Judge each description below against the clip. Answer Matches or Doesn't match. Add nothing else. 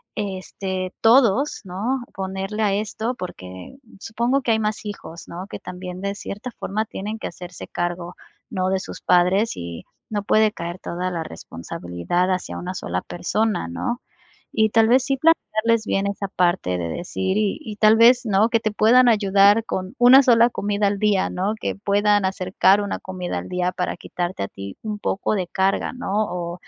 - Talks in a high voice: Matches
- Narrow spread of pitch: Doesn't match